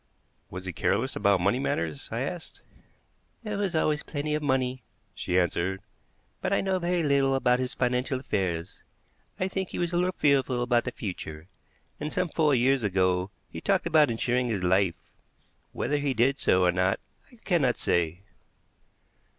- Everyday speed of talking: Yes, average, 170 wpm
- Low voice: Yes, low, 125 Hz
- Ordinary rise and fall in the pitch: No, wide, 8.0 semitones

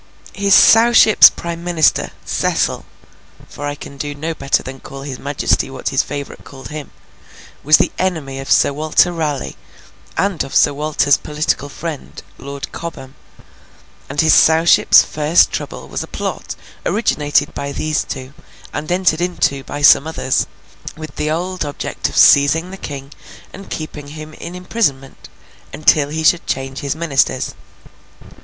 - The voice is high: No, medium, 150 Hz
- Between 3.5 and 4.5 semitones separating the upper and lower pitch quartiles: No, average, 3.1 semitones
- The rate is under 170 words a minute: Yes, average, 150 wpm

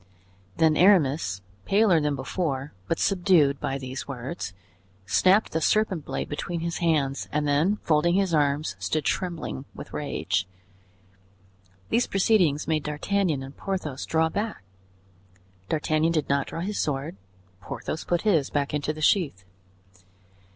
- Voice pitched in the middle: Yes, medium, 155 Hz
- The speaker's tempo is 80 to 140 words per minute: Yes, slow, 135 wpm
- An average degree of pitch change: Yes, average, 4.1 semitones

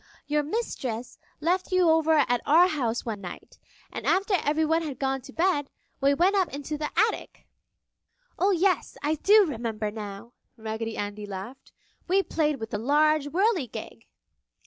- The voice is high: Yes, very high, 295 Hz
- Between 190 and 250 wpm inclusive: No, average, 155 wpm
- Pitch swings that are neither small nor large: No, wide, 6.8 semitones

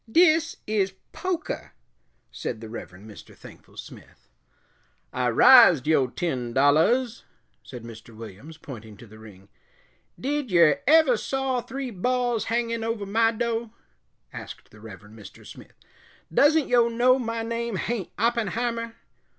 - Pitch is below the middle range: No, high, 225 Hz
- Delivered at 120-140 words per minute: Yes, slow, 135 wpm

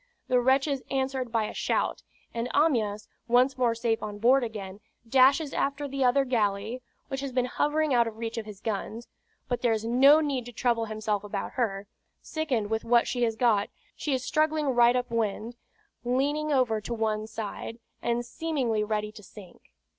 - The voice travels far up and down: No, average, 3.4 semitones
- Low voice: No, high, 240 Hz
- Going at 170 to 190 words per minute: Yes, average, 185 wpm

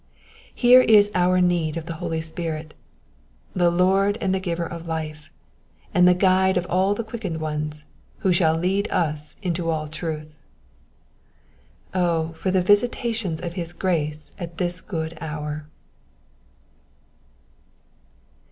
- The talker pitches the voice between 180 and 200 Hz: No, medium, 170 Hz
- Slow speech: Yes, slow, 130 wpm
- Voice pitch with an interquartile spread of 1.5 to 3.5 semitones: Yes, average, 2.8 semitones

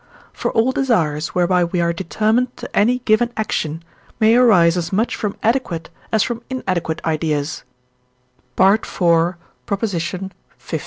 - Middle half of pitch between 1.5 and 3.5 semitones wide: No, average, 5.2 semitones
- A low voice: No, high, 190 Hz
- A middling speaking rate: No, slow, 125 wpm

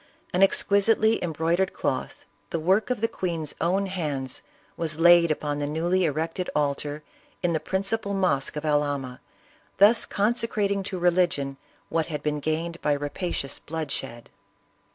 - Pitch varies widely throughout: No, average, 4.3 semitones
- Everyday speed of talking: Yes, average, 145 wpm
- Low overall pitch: No, medium, 165 Hz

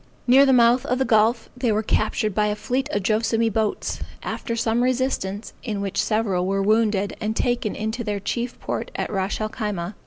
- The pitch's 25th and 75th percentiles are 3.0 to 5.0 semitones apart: No, narrow, 2.5 semitones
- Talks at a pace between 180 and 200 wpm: Yes, average, 195 wpm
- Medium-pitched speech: No, high, 220 Hz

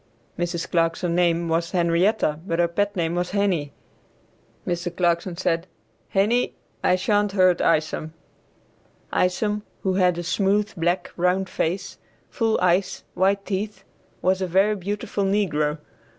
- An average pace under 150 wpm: Yes, slow, 135 wpm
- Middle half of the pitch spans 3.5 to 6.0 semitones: No, average, 2.7 semitones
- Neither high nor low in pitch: Yes, medium, 180 Hz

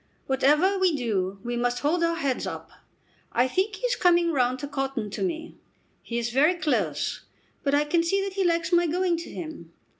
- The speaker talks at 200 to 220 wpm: Yes, fast, 205 wpm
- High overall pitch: Yes, very high, 300 Hz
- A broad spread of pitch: Yes, wide, 5.9 semitones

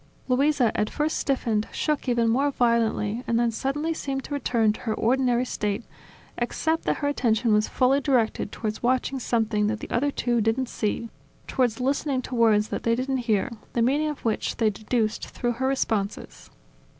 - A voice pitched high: Yes, high, 240 Hz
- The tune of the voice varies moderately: Yes, average, 3.2 semitones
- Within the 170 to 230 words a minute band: Yes, average, 180 wpm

